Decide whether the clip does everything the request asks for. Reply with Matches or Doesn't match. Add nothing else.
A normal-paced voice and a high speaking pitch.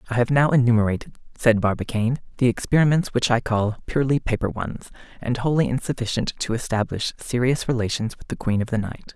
Doesn't match